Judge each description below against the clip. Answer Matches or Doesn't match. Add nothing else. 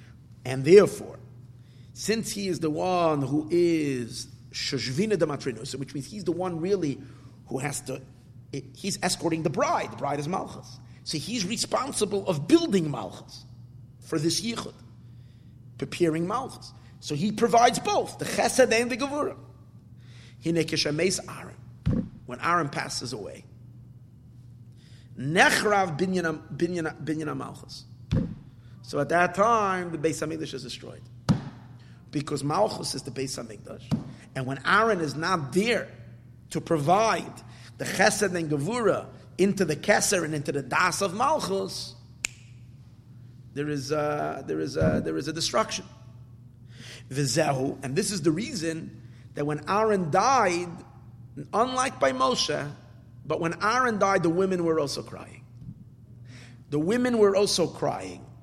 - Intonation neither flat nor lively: Doesn't match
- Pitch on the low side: Doesn't match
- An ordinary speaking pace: Doesn't match